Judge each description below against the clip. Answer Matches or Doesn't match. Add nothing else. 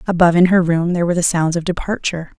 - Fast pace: Matches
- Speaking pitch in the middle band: Matches